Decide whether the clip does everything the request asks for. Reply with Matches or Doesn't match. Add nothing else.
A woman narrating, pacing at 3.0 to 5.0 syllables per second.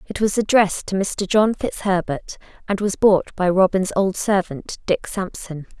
Matches